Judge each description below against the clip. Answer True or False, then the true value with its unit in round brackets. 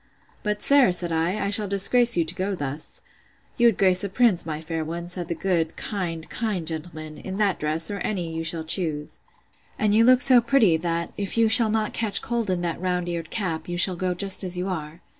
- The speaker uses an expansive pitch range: False (4.1 semitones)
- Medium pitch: True (180 Hz)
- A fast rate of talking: True (225 wpm)